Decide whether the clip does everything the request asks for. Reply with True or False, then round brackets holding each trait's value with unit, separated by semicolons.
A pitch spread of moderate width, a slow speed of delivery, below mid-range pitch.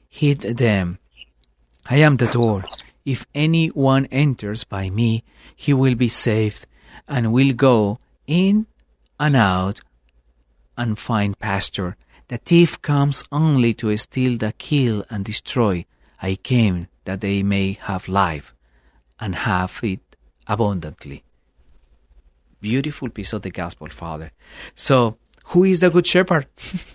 False (6.5 semitones; 130 wpm; 110 Hz)